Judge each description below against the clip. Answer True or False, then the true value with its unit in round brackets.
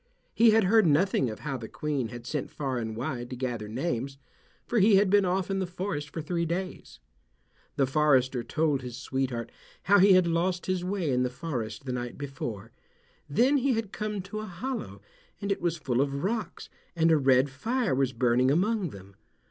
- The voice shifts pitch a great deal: True (7.0 semitones)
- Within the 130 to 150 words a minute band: False (200 wpm)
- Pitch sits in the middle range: True (150 Hz)